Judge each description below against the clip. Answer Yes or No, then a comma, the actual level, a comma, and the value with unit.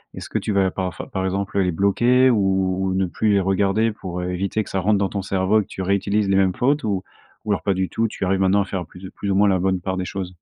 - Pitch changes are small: Yes, narrow, 1.4 semitones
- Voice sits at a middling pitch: No, very low, 95 Hz